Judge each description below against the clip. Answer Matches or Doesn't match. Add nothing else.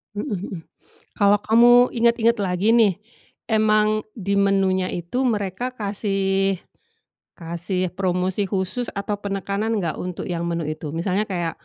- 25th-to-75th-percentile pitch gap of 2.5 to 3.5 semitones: Matches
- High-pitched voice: Matches